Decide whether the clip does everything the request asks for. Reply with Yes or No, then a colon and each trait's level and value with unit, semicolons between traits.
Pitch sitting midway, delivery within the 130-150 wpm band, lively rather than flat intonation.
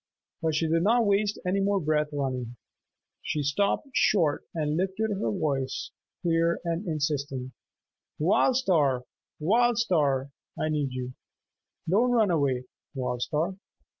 Yes: medium, 160 Hz; slow, 135 wpm; wide, 5.9 semitones